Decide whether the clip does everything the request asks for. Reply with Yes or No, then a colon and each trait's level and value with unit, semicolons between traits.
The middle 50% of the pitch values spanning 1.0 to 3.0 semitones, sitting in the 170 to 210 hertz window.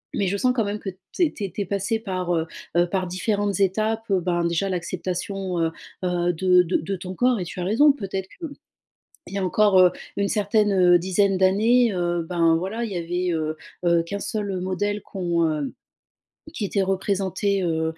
Yes: narrow, 2.6 semitones; high, 190 Hz